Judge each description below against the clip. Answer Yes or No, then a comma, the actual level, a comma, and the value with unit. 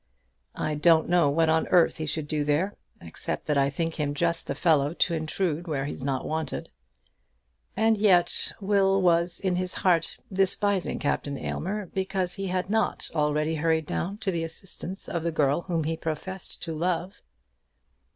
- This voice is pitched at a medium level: Yes, medium, 170 Hz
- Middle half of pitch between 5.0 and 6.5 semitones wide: No, average, 3.5 semitones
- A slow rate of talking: No, average, 175 wpm